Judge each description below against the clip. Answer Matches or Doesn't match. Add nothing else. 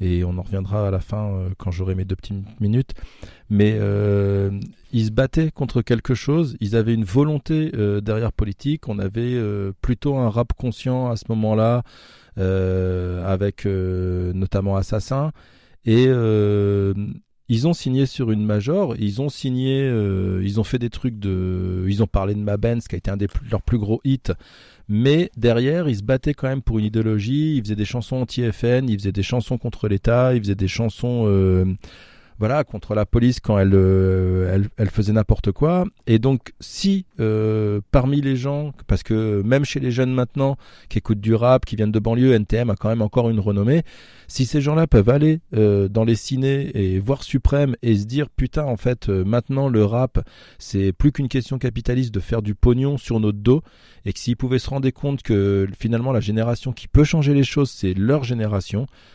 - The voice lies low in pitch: Matches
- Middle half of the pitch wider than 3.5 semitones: Matches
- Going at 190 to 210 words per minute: Matches